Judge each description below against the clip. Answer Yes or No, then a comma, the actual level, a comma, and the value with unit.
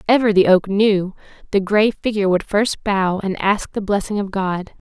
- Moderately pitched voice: No, high, 200 Hz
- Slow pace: No, average, 195 wpm